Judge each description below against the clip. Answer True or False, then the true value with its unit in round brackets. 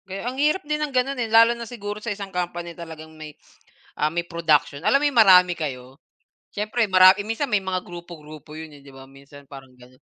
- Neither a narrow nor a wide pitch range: False (6.4 semitones)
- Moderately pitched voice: True (175 Hz)